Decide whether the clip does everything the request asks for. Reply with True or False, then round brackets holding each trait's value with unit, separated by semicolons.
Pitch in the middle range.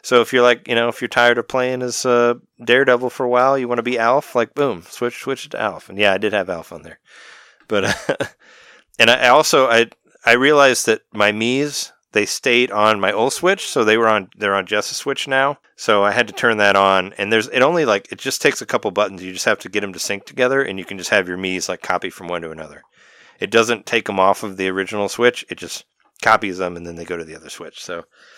False (115 Hz)